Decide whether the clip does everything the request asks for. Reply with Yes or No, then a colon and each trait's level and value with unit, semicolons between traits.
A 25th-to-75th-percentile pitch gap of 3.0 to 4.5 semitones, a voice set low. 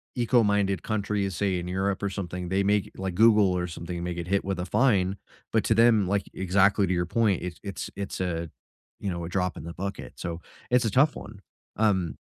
No: narrow, 2.5 semitones; very low, 95 Hz